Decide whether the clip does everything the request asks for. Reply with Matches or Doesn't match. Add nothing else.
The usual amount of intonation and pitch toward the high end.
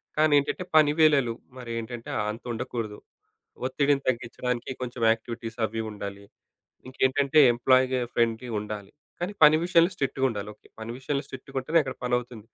Doesn't match